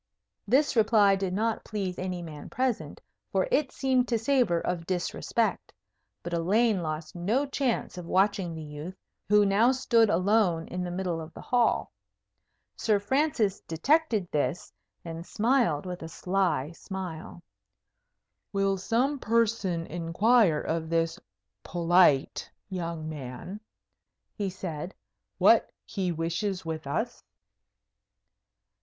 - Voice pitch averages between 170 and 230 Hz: Yes, medium, 185 Hz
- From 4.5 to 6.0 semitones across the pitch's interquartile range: Yes, average, 5.2 semitones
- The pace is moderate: No, slow, 125 wpm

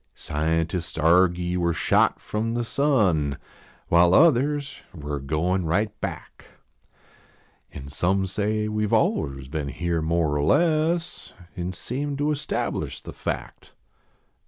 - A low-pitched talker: Yes, very low, 90 Hz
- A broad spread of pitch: Yes, wide, 6.8 semitones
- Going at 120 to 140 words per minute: Yes, slow, 135 wpm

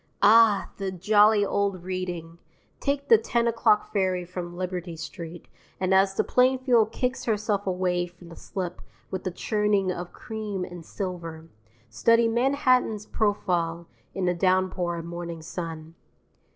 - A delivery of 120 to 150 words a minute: Yes, average, 140 wpm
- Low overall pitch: No, medium, 185 Hz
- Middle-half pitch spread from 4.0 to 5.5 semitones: No, average, 3.5 semitones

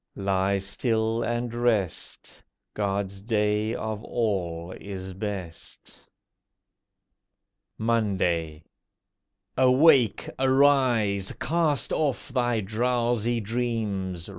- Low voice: Yes, low, 110 Hz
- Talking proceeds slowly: Yes, slow, 75 wpm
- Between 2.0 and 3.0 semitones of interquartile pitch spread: No, average, 3.8 semitones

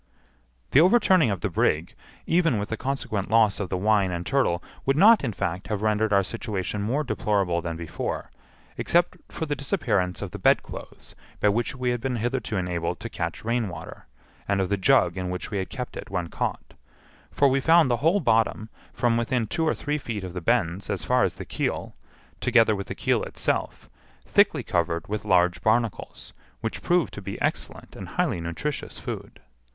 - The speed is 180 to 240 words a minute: Yes, average, 190 wpm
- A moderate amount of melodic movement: No, wide, 5.7 semitones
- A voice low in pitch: Yes, low, 110 Hz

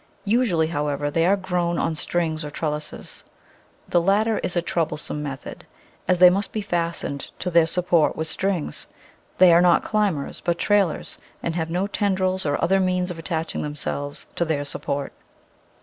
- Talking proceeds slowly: No, average, 165 wpm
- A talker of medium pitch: Yes, medium, 170 Hz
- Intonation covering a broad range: No, average, 3.0 semitones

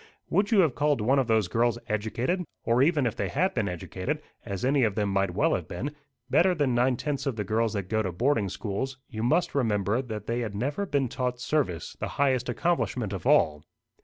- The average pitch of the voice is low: Yes, low, 120 Hz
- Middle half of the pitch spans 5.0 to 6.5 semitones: Yes, average, 5.3 semitones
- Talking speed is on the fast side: Yes, fast, 220 wpm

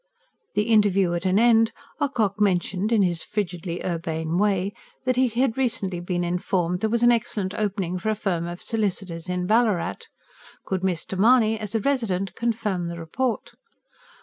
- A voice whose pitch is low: No, high, 195 Hz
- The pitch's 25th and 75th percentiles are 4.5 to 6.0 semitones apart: No, average, 3.9 semitones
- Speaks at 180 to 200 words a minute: No, average, 165 wpm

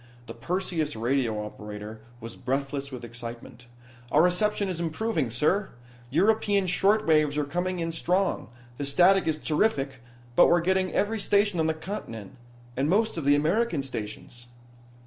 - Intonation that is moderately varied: No, wide, 6.5 semitones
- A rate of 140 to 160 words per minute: Yes, average, 150 wpm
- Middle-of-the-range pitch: Yes, medium, 155 Hz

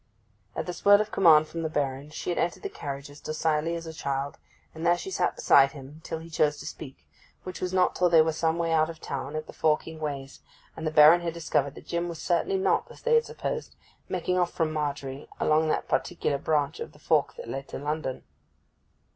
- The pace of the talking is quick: Yes, fast, 230 wpm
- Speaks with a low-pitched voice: No, medium, 160 Hz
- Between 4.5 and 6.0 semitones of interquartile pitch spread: No, average, 2.8 semitones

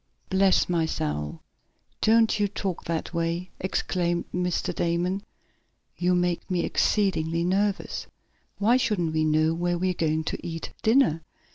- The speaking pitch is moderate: Yes, medium, 175 Hz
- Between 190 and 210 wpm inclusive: No, average, 140 wpm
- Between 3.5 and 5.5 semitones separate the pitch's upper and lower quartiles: No, narrow, 2.6 semitones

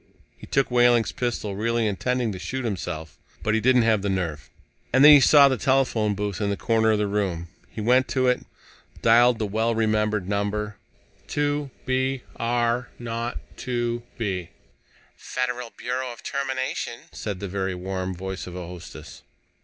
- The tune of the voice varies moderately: Yes, average, 3.8 semitones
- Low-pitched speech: Yes, low, 115 Hz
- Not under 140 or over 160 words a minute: No, average, 170 wpm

